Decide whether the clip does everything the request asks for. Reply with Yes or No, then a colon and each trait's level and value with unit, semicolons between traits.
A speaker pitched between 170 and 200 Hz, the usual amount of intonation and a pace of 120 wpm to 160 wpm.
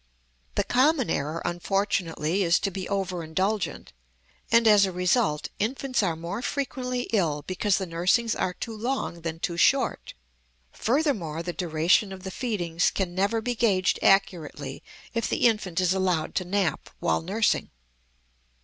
Yes: high, 190 Hz; average, 4.6 semitones; average, 150 wpm